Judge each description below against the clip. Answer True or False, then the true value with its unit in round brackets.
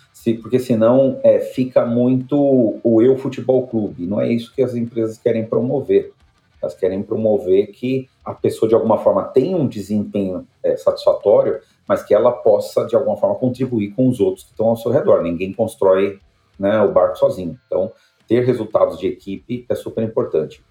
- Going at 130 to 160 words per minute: False (175 wpm)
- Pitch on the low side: True (125 Hz)